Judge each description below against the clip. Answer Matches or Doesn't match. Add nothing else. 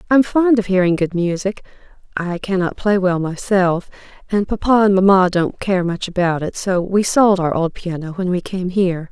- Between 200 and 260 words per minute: Matches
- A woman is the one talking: Matches